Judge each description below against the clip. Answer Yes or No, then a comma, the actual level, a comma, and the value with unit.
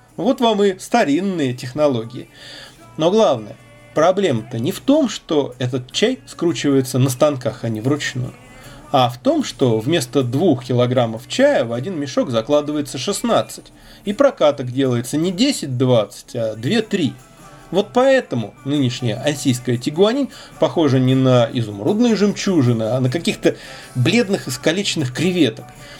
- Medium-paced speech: Yes, average, 130 wpm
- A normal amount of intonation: No, wide, 7.4 semitones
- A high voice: No, medium, 140 Hz